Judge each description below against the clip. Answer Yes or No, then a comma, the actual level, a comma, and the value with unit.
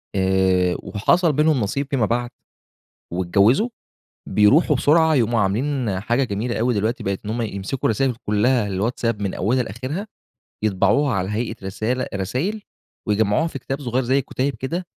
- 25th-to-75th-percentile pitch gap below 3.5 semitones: No, average, 4.9 semitones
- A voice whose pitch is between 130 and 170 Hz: No, low, 120 Hz